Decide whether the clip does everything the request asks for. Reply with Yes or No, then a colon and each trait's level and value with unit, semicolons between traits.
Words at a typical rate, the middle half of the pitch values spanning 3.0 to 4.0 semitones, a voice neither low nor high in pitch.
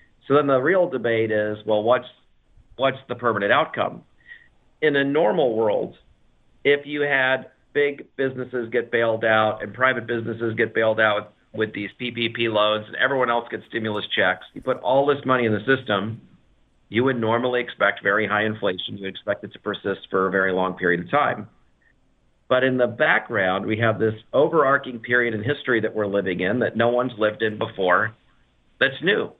No: average, 185 wpm; average, 3.4 semitones; low, 115 Hz